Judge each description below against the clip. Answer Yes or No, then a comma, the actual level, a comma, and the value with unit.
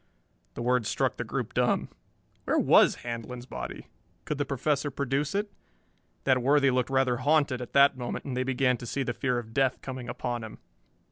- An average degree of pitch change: No, narrow, 2.2 semitones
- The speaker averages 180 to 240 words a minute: Yes, average, 190 wpm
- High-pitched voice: No, low, 130 Hz